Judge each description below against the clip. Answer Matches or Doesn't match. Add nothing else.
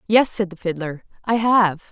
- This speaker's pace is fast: Doesn't match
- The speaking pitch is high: Matches